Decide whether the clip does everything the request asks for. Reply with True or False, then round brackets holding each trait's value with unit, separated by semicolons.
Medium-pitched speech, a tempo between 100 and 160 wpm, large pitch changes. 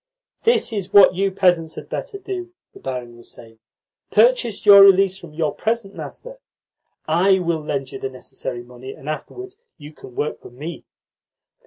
False (175 Hz; 170 wpm; 7.0 semitones)